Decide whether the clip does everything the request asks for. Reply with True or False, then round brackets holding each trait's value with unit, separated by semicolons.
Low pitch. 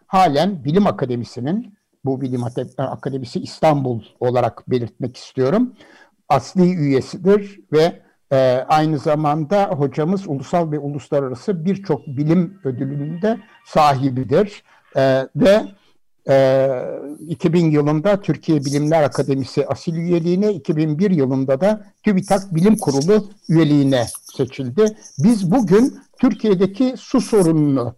False (155 Hz)